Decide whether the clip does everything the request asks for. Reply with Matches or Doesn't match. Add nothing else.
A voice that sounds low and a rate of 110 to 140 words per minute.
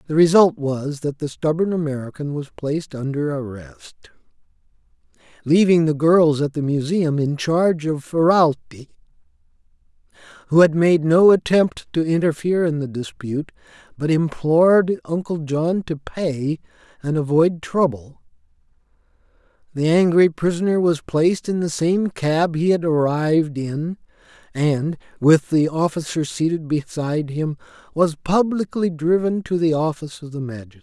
Doesn't match